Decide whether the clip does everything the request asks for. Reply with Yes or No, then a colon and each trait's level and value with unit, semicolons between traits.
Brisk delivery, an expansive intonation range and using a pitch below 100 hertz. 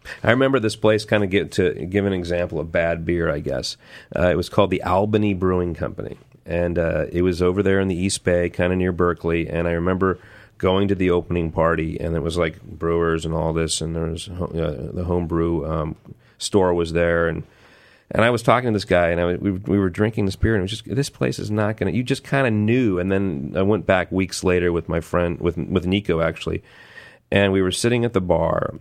No: fast, 240 wpm; average, 3.2 semitones; very low, 90 Hz